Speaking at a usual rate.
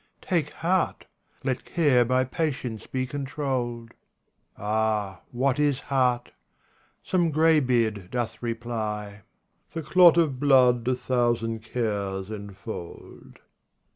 No: slow, 105 wpm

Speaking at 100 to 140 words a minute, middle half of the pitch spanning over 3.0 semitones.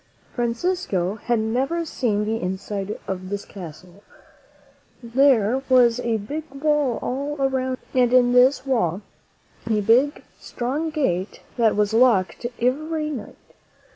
Yes: slow, 135 wpm; average, 4.6 semitones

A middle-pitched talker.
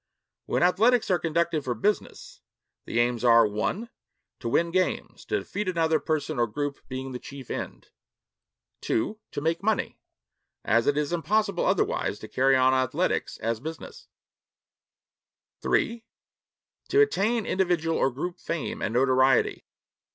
Yes: medium, 160 Hz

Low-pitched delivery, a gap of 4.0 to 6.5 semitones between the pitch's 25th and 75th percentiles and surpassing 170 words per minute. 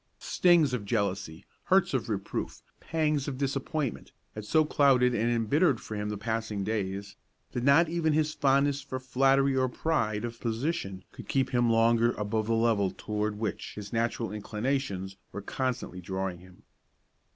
No: low, 115 Hz; average, 4.7 semitones; average, 160 wpm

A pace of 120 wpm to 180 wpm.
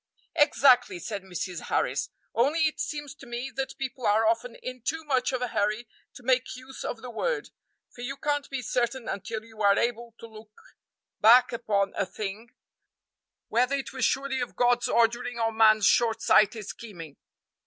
Yes: average, 175 wpm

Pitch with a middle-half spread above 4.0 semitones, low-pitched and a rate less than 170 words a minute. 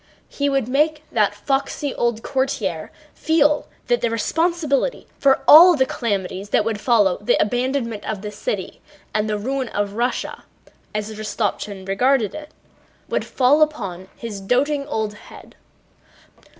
No: average, 5.1 semitones; high, 240 Hz; average, 140 wpm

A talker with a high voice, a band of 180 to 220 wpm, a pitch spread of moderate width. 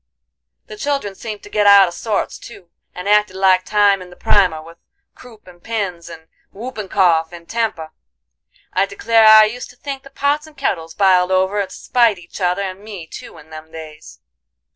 Yes: high, 195 Hz; average, 190 wpm; average, 4.0 semitones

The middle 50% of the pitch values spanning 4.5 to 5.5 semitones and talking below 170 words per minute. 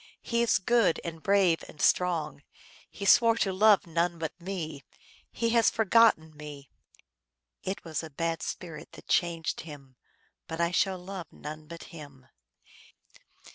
No: average, 3.8 semitones; average, 145 wpm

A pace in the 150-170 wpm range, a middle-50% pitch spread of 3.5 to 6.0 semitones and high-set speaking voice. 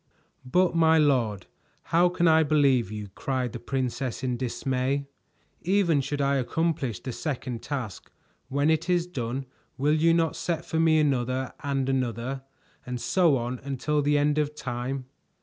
No: average, 160 wpm; average, 3.9 semitones; medium, 140 Hz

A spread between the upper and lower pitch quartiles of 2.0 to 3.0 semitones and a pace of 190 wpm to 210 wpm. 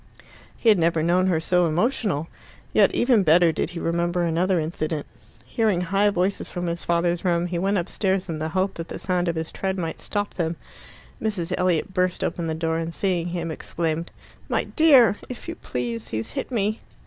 Yes: average, 2.7 semitones; average, 195 wpm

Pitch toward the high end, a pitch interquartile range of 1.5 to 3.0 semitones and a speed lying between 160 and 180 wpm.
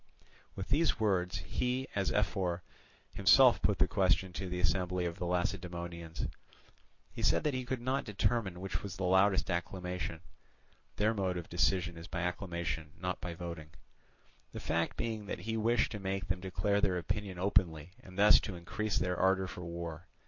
No: very low, 90 Hz; narrow, 2.6 semitones; average, 175 wpm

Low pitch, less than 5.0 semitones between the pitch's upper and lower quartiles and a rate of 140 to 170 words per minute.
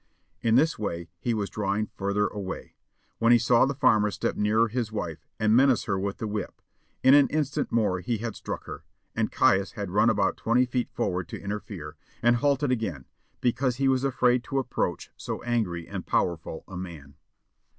No: low, 110 Hz; average, 4.2 semitones; average, 190 wpm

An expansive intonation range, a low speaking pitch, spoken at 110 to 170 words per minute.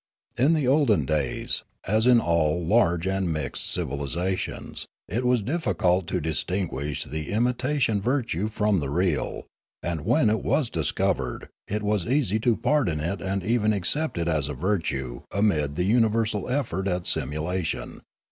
Yes: wide, 5.9 semitones; very low, 95 Hz; average, 150 wpm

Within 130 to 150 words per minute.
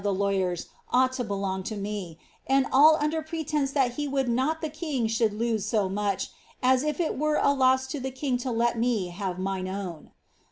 No: fast, 205 wpm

